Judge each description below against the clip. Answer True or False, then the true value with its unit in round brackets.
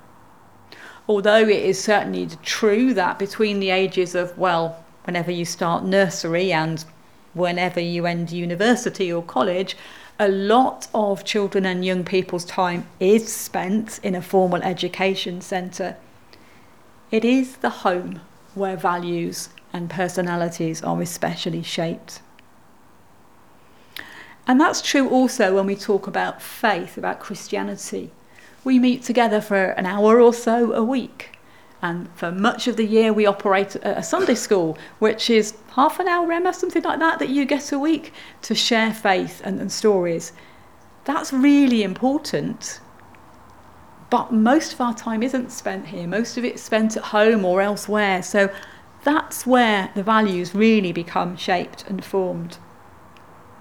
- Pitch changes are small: False (4.4 semitones)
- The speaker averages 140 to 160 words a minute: True (145 wpm)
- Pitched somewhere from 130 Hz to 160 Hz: False (200 Hz)